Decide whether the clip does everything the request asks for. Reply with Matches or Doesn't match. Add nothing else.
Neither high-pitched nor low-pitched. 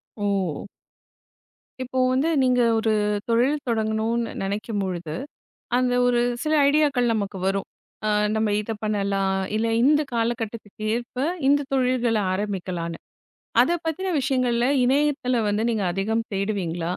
Doesn't match